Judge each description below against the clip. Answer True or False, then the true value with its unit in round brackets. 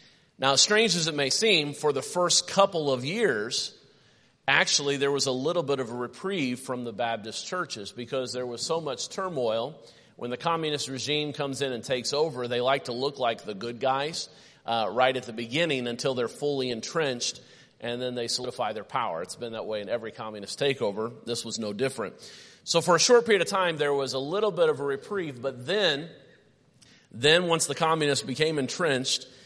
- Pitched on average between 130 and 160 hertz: True (135 Hz)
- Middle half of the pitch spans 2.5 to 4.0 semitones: False (4.7 semitones)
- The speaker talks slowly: False (200 wpm)